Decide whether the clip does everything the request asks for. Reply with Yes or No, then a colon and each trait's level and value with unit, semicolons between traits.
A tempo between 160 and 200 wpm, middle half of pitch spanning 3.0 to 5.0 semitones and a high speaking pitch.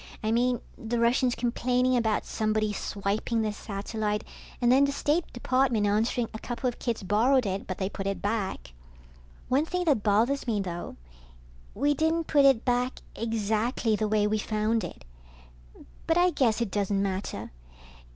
Yes: average, 165 wpm; average, 3.4 semitones; high, 225 Hz